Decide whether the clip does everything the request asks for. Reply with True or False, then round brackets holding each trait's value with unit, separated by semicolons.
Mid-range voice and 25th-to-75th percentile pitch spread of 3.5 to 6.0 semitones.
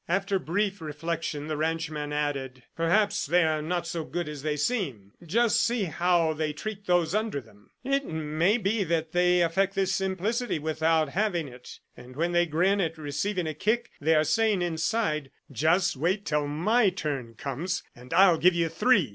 True (165 Hz; 4.2 semitones)